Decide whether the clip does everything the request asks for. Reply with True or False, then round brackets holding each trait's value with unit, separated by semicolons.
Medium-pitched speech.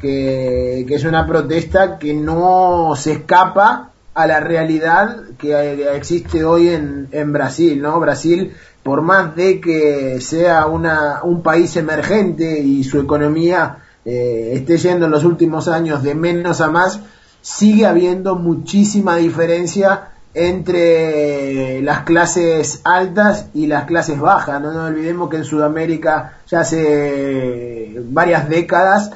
True (160 Hz)